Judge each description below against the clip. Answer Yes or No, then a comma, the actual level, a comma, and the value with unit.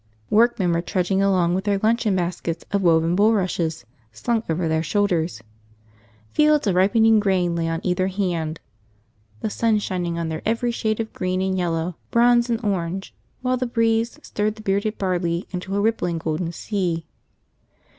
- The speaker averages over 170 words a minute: No, average, 165 wpm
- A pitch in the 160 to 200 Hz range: Yes, high, 190 Hz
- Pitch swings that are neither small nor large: Yes, average, 4.2 semitones